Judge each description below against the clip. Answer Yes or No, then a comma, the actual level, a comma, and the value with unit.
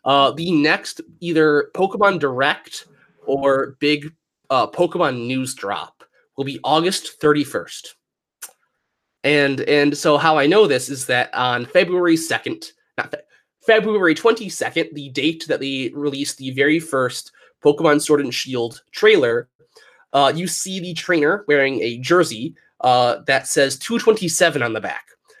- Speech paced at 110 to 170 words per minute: Yes, average, 140 wpm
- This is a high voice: No, medium, 150 Hz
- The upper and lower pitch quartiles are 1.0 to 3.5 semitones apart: No, average, 4.3 semitones